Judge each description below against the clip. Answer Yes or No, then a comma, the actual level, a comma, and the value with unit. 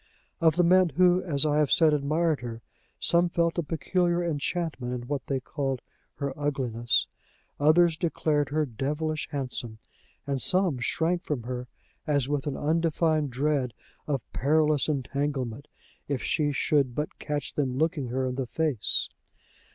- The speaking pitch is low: No, medium, 145 Hz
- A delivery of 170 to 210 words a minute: No, average, 155 wpm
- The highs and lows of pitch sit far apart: No, average, 3.4 semitones